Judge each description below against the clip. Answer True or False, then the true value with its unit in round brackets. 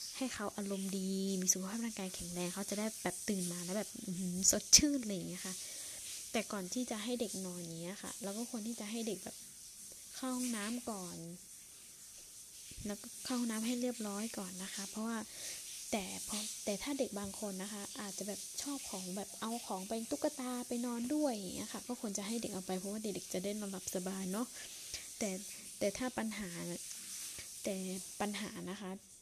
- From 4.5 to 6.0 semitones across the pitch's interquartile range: False (3.5 semitones)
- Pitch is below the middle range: False (205 Hz)